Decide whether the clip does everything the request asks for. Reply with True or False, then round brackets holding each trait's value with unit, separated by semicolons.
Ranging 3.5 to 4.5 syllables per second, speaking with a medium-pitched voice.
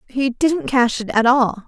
False (4.0 syllables/s; 245 Hz)